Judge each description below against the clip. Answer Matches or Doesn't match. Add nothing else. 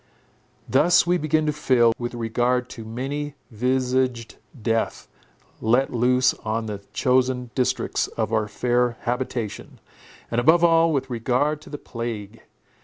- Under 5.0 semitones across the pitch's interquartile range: Matches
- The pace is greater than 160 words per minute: Doesn't match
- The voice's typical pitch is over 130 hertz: Doesn't match